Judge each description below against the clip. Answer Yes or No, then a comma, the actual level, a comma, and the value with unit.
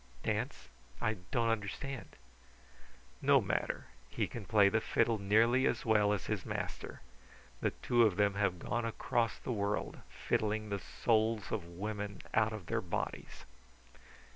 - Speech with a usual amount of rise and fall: No, narrow, 2.1 semitones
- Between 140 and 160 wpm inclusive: Yes, average, 145 wpm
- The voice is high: No, low, 110 Hz